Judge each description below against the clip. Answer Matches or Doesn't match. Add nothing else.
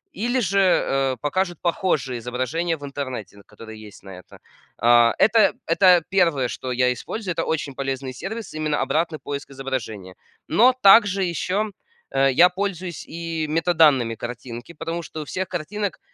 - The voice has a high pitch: Doesn't match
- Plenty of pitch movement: Matches